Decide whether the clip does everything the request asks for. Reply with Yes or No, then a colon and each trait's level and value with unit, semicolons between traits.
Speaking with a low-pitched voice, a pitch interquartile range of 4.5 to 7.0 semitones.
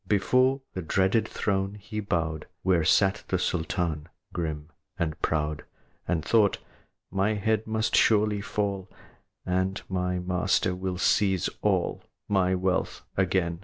No: very low, 95 Hz; narrow, 2.6 semitones